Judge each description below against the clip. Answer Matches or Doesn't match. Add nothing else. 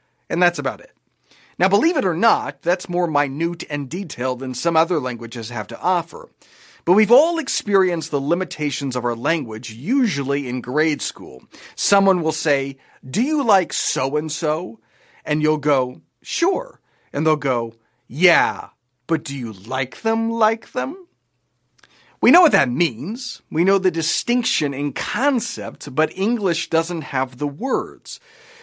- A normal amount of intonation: Doesn't match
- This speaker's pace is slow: Doesn't match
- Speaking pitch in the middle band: Matches